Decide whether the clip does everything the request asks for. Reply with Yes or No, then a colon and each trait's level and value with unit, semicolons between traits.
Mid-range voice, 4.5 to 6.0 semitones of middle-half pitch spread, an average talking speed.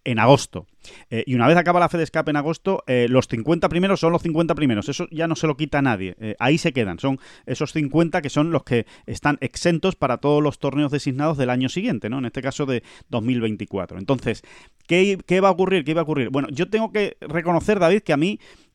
No: medium, 150 Hz; average, 4.9 semitones; fast, 240 wpm